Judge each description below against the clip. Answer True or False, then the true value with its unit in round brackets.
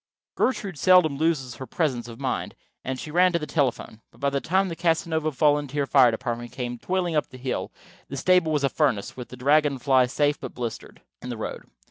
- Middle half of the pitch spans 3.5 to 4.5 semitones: True (4.2 semitones)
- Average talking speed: False (210 wpm)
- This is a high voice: False (140 Hz)